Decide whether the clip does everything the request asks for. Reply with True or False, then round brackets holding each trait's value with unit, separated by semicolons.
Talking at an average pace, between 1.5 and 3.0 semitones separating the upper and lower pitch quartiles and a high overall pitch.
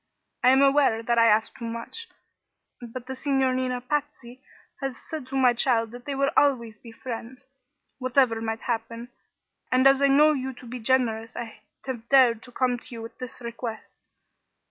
True (180 wpm; 2.5 semitones; 250 Hz)